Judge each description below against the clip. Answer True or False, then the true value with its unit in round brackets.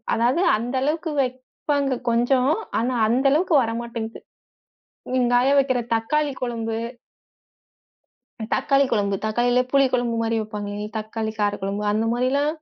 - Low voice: False (245 Hz)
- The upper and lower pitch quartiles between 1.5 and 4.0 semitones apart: True (3.4 semitones)